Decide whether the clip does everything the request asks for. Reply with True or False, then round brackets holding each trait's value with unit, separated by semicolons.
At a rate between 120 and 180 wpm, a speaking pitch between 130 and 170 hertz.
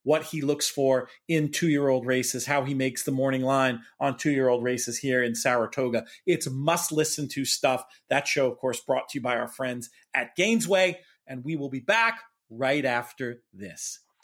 False (200 wpm; 135 Hz)